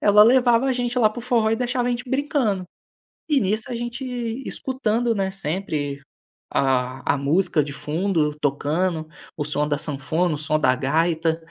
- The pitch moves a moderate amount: No, wide, 8.1 semitones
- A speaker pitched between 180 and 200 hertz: Yes, high, 190 Hz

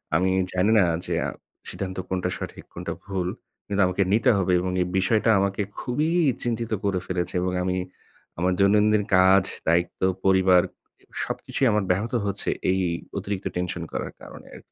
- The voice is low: Yes, very low, 95 Hz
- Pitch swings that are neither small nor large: No, narrow, 2.1 semitones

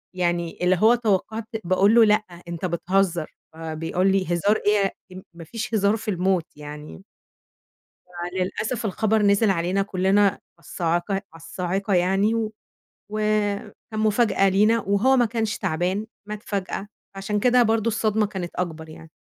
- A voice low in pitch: No, high, 195 Hz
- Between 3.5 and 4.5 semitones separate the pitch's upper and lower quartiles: No, average, 3.1 semitones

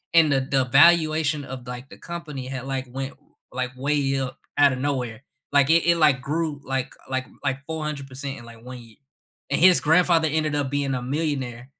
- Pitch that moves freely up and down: No, average, 2.9 semitones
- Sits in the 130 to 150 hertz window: Yes, low, 135 Hz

